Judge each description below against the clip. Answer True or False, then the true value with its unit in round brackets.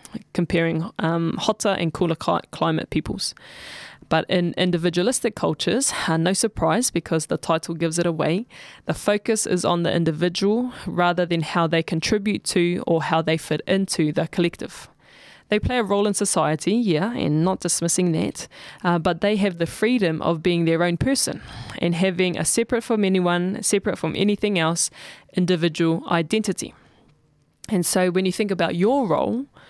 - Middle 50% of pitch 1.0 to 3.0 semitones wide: False (3.4 semitones)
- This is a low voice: False (175 Hz)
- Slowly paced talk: False (160 wpm)